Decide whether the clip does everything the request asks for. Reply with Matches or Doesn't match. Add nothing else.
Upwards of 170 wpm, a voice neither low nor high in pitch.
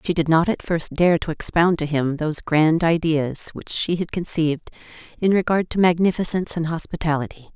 Matches